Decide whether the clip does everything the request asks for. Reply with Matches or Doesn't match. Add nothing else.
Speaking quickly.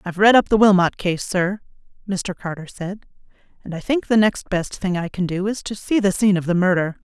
Matches